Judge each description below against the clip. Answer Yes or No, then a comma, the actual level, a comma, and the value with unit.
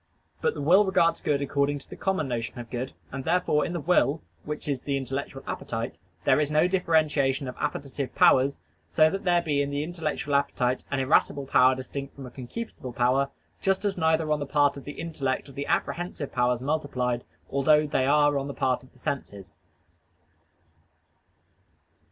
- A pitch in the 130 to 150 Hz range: Yes, medium, 140 Hz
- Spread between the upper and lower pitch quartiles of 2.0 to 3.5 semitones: Yes, average, 3.0 semitones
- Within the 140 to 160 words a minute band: No, average, 185 wpm